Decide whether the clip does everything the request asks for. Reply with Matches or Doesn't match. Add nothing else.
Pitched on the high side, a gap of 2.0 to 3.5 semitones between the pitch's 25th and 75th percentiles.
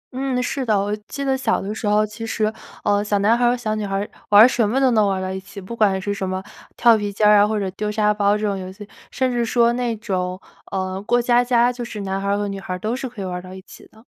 Matches